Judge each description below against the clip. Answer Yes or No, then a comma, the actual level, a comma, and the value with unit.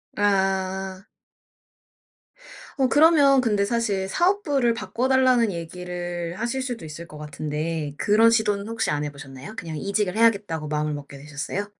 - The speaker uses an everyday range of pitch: No, wide, 6.4 semitones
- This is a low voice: No, high, 195 Hz